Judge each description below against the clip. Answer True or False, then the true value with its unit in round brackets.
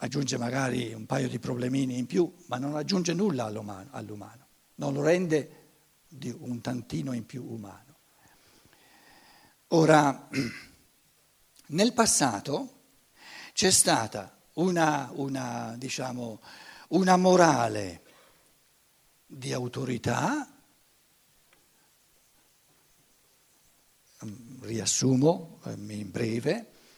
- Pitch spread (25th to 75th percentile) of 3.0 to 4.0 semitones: False (5.4 semitones)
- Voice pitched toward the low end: True (130 Hz)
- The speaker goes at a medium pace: False (80 wpm)